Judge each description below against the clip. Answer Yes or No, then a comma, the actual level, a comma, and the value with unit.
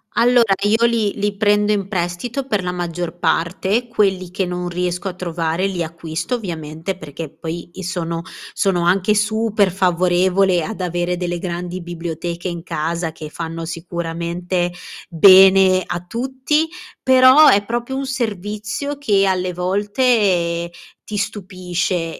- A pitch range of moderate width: Yes, average, 3.3 semitones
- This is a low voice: No, medium, 185 Hz